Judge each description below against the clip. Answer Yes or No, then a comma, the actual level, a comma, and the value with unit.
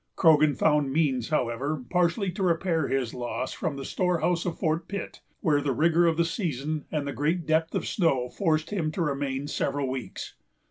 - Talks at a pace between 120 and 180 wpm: No, average, 190 wpm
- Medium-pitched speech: Yes, medium, 155 Hz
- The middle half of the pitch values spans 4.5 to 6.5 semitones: No, average, 3.5 semitones